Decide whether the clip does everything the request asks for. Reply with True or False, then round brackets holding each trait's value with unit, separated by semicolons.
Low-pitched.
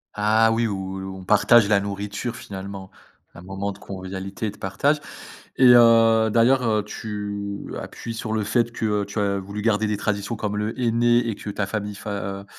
True (105 Hz)